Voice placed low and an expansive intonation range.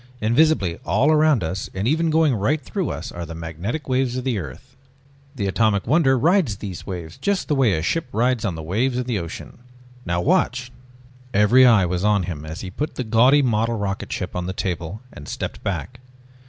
Yes: low, 110 Hz; wide, 6.5 semitones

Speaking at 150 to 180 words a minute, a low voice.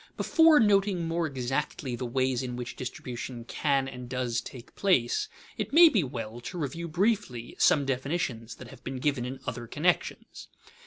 Yes: average, 170 wpm; low, 130 Hz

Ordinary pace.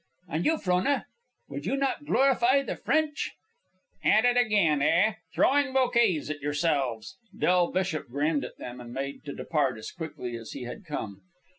Yes: average, 165 wpm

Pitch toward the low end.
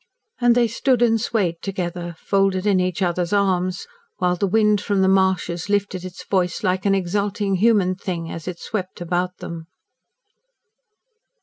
No: high, 190 Hz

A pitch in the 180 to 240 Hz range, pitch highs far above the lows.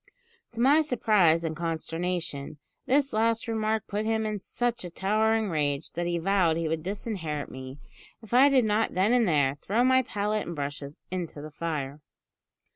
Yes: high, 190 Hz; wide, 5.7 semitones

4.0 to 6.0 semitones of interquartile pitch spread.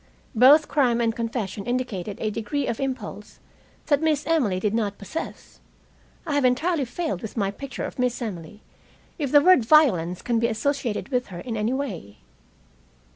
Yes: average, 5.1 semitones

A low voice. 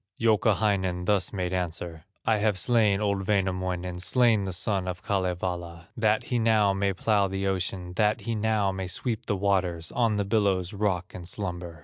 Yes: very low, 95 Hz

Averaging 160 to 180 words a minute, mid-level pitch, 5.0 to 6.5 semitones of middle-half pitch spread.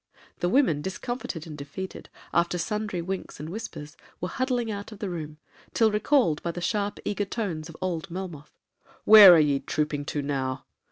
Yes: average, 170 wpm; medium, 180 Hz; wide, 5.4 semitones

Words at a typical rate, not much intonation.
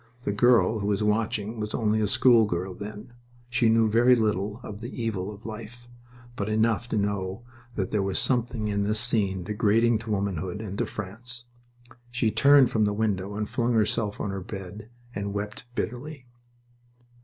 Yes: average, 175 wpm; narrow, 2.3 semitones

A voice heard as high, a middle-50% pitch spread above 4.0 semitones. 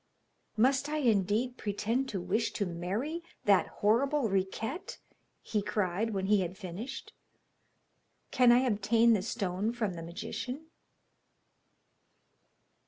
Yes: high, 215 Hz; average, 4.4 semitones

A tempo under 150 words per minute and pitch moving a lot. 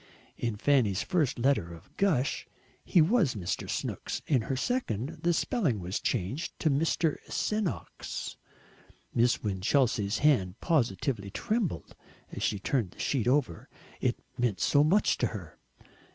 Yes: average, 140 wpm; wide, 7.6 semitones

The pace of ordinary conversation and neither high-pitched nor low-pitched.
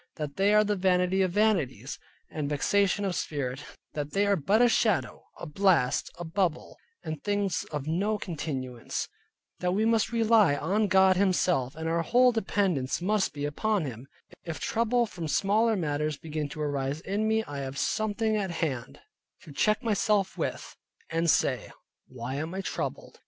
Yes: average, 170 wpm; medium, 180 Hz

